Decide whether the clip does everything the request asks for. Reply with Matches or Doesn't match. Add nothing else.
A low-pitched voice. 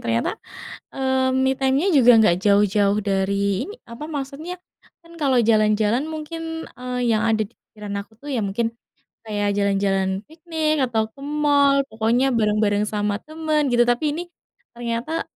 Doesn't match